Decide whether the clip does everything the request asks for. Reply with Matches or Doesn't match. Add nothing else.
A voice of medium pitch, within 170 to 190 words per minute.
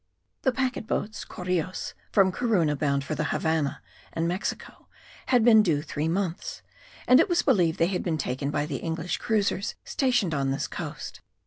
Matches